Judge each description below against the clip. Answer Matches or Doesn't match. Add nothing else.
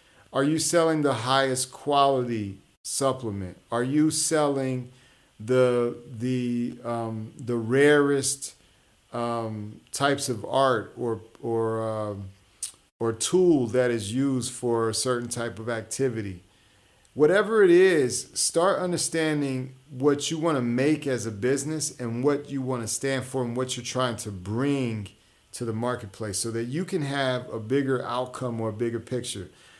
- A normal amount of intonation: Matches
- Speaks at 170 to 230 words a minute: Doesn't match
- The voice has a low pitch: Matches